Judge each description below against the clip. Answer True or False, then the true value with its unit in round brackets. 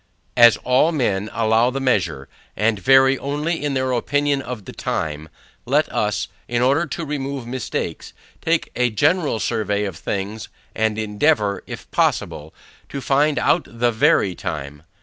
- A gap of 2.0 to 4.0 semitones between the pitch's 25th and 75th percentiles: False (4.9 semitones)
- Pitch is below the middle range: True (120 Hz)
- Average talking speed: True (150 wpm)